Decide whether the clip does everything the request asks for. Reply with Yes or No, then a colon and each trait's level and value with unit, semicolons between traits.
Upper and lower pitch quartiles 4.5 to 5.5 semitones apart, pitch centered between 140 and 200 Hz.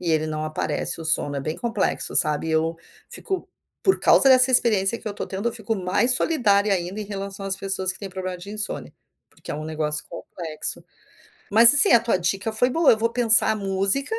Yes: average, 5.0 semitones; high, 195 Hz